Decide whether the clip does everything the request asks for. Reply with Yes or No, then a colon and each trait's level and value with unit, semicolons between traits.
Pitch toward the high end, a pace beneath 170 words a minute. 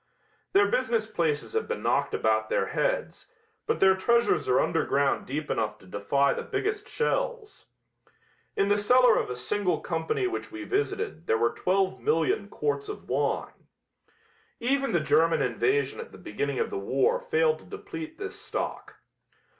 Yes: very high, 255 Hz; average, 160 wpm